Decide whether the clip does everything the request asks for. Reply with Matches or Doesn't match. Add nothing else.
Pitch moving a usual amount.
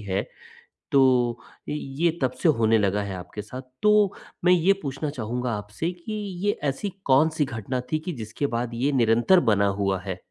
Doesn't match